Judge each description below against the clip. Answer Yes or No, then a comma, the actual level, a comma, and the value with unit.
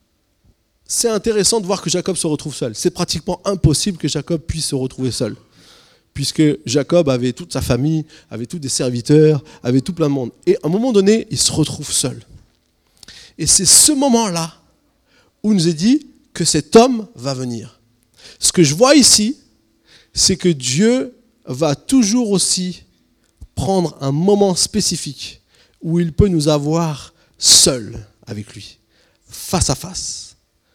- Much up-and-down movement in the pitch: Yes, wide, 7.0 semitones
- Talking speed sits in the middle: Yes, average, 160 wpm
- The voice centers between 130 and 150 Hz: No, medium, 160 Hz